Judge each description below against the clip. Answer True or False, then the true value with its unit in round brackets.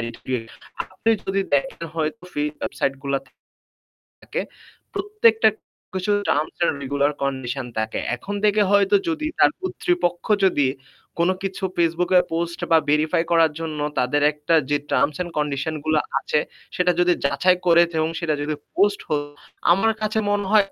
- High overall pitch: False (165 Hz)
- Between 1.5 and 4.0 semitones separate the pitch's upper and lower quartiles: False (5.0 semitones)